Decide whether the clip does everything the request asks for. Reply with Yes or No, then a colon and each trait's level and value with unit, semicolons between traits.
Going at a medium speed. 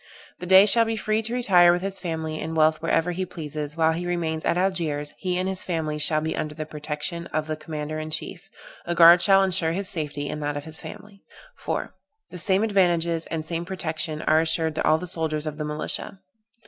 No: fast, 220 wpm